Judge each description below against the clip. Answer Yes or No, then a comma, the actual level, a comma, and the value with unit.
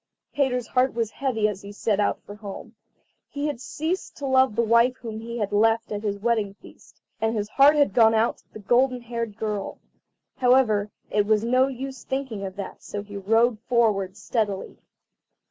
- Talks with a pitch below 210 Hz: No, high, 225 Hz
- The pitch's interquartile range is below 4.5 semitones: Yes, average, 3.3 semitones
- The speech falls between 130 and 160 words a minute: No, average, 190 wpm